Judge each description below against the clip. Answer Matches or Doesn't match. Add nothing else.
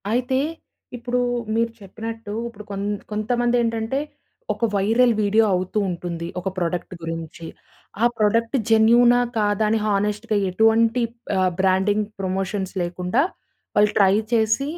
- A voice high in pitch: Matches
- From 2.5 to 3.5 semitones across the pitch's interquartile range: Matches